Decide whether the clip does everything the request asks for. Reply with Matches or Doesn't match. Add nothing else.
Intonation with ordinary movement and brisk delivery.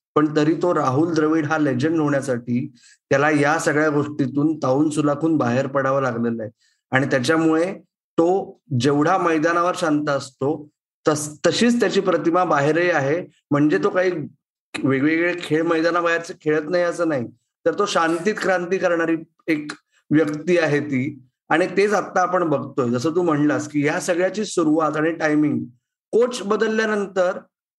Matches